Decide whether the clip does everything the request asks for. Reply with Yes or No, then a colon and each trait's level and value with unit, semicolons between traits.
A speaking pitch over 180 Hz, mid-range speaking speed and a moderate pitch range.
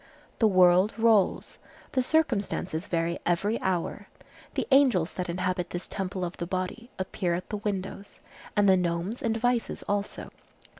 Yes: high, 190 Hz; average, 150 wpm; average, 3.4 semitones